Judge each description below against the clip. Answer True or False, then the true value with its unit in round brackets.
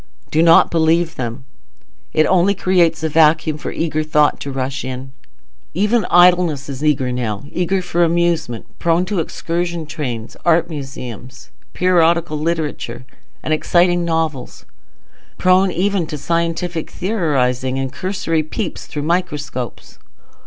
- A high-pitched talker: False (160 Hz)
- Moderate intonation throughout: True (3.6 semitones)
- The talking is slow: True (125 wpm)